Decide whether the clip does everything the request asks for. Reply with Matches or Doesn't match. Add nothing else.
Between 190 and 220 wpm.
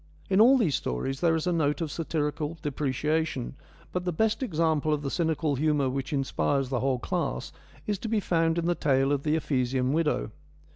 Matches